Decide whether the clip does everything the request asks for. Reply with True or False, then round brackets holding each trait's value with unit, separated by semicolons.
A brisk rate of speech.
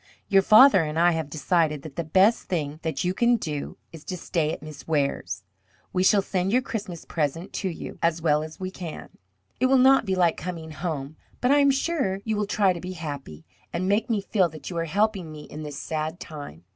True (225 wpm)